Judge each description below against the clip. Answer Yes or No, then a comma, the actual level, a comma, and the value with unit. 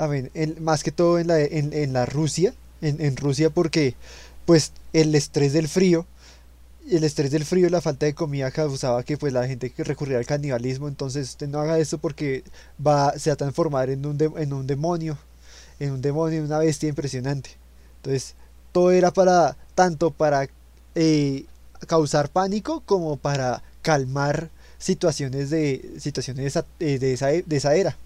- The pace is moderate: Yes, average, 180 wpm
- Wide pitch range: No, average, 3.1 semitones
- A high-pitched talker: No, medium, 150 Hz